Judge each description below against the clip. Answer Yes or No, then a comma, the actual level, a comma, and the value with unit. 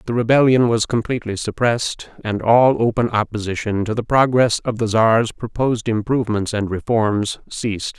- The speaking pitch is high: No, low, 115 Hz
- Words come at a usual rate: Yes, average, 150 wpm